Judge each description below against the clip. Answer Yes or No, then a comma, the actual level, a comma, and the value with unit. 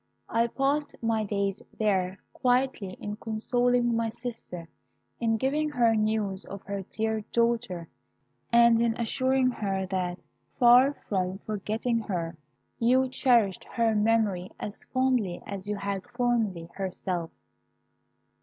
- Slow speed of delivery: Yes, slow, 125 wpm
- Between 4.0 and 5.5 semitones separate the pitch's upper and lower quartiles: No, average, 3.6 semitones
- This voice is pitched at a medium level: No, high, 220 Hz